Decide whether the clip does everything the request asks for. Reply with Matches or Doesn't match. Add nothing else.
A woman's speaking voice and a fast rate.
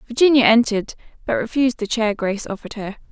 Doesn't match